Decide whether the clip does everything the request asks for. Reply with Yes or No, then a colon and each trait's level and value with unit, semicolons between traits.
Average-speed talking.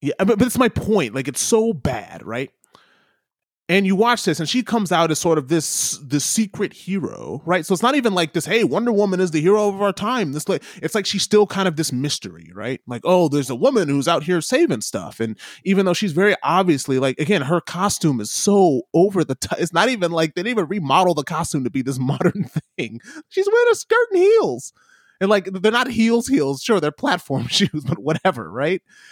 No: fast, 230 wpm